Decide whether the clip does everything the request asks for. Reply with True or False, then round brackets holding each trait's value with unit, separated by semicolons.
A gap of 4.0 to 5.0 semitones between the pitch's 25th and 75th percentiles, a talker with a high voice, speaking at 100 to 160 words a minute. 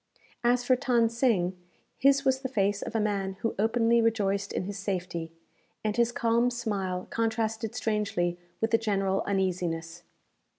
False (3.4 semitones; 215 Hz; 155 wpm)